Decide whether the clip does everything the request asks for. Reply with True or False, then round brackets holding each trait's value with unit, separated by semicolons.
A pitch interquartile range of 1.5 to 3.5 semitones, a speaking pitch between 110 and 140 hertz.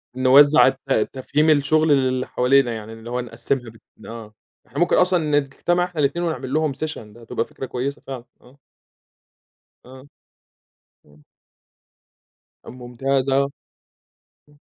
True (3.1 semitones; 135 Hz)